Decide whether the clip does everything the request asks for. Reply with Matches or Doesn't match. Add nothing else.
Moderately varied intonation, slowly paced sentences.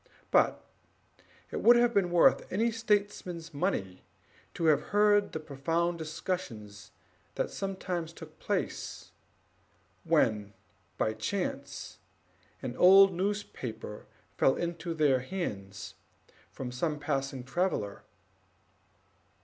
Doesn't match